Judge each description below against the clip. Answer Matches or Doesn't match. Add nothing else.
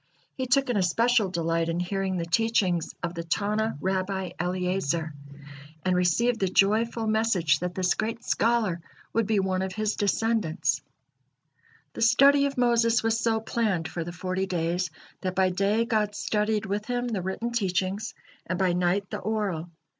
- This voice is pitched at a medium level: Doesn't match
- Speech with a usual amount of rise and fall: Matches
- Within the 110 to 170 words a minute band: Matches